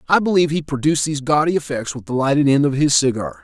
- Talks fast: Yes, fast, 245 wpm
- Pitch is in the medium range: Yes, medium, 145 Hz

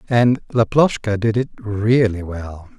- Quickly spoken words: No, slow, 130 wpm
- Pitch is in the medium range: No, low, 110 Hz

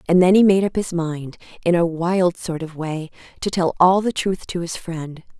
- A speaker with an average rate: No, fast, 235 wpm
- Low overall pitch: No, medium, 175 Hz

